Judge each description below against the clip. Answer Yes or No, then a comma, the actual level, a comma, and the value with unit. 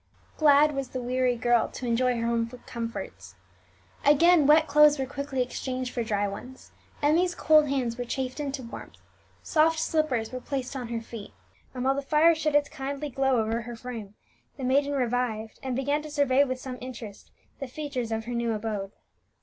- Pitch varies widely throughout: No, average, 3.4 semitones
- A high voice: Yes, very high, 255 Hz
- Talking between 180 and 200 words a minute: Yes, average, 185 wpm